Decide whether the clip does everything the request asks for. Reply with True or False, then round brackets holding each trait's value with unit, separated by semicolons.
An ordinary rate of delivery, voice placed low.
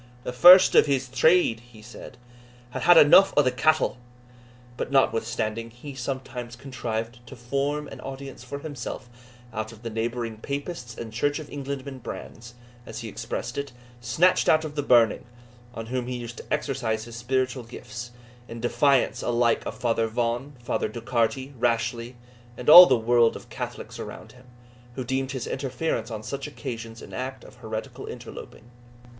True (165 wpm; 125 Hz)